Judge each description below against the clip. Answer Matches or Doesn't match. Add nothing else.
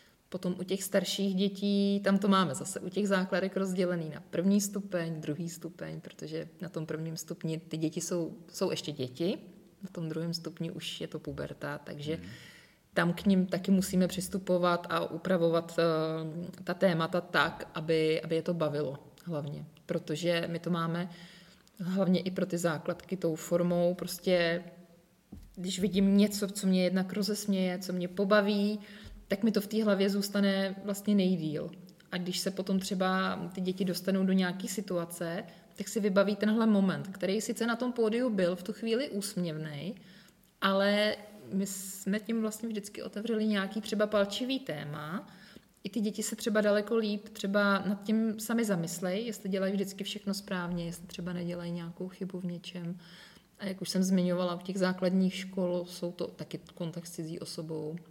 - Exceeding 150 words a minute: Matches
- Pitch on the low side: Doesn't match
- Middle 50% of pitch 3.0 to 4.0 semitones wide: Doesn't match